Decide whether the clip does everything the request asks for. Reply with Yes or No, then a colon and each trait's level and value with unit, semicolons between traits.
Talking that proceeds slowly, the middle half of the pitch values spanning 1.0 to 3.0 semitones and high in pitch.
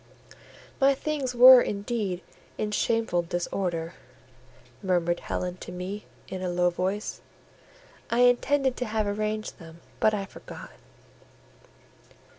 No: slow, 115 wpm; average, 4.9 semitones; high, 205 Hz